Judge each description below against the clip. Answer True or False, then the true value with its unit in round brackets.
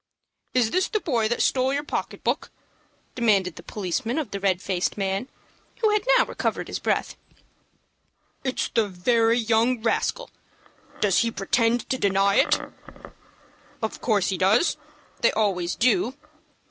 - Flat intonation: False (4.5 semitones)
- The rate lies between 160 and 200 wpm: False (145 wpm)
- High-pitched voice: True (225 Hz)